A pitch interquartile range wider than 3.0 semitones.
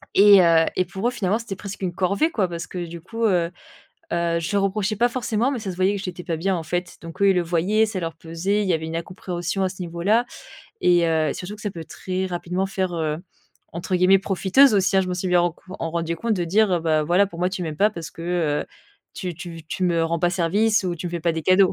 No: average, 2.7 semitones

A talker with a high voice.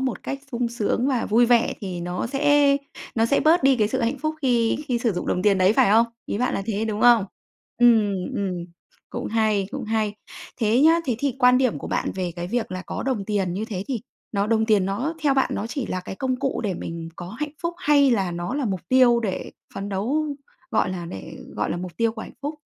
Yes: high, 225 Hz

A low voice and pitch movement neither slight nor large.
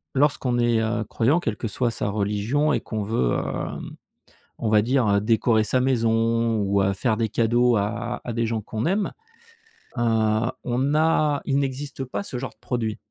Yes: low, 115 Hz; average, 3.1 semitones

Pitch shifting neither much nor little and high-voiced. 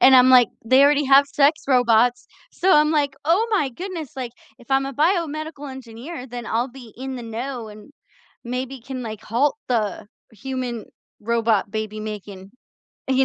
Yes: average, 3.6 semitones; very high, 255 Hz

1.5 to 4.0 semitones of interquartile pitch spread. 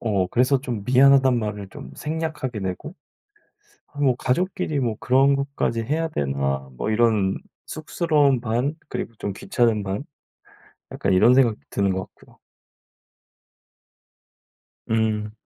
No: average, 5.1 semitones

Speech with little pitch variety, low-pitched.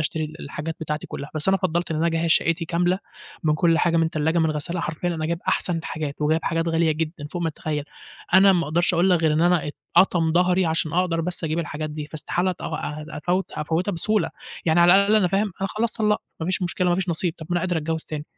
No: narrow, 2.2 semitones; medium, 165 Hz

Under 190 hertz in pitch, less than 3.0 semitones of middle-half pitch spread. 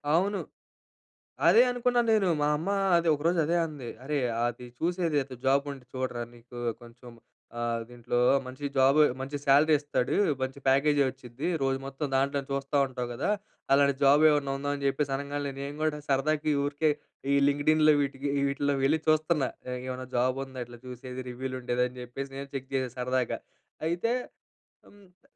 Yes: medium, 140 Hz; narrow, 2.6 semitones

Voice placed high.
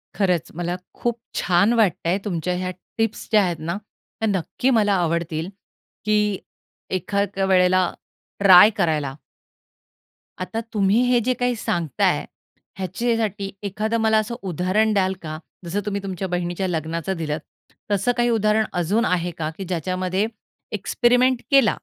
Yes: high, 195 Hz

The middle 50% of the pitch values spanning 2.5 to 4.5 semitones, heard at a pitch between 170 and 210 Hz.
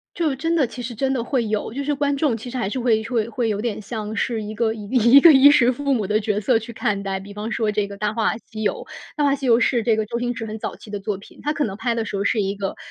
No: average, 3.5 semitones; high, 230 Hz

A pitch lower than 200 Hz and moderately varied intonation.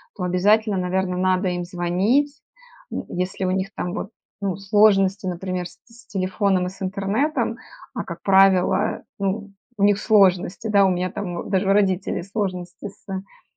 No: high, 190 Hz; narrow, 2.0 semitones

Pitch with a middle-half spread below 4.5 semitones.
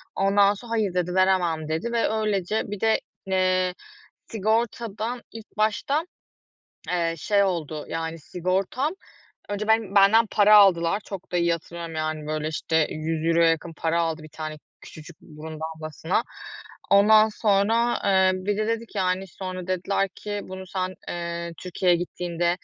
Yes: average, 3.8 semitones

